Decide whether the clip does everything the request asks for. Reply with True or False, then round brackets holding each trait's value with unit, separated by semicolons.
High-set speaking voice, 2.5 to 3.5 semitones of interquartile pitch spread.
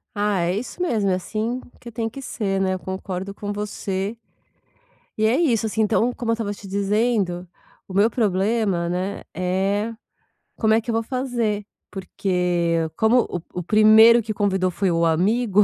True (205 Hz; 3.1 semitones)